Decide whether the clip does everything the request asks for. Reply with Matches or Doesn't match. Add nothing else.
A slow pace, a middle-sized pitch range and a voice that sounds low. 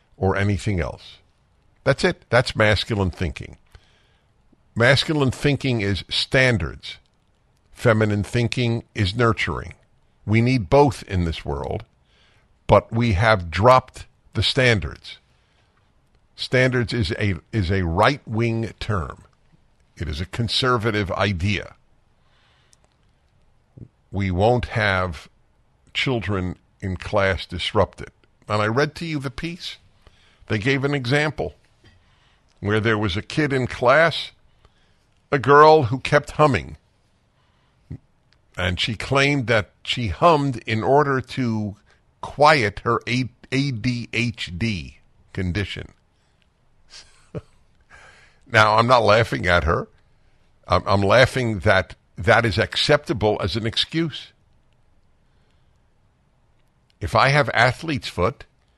Matches